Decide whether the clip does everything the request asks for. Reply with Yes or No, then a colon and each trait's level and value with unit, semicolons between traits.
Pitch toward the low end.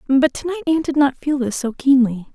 No: very high, 275 Hz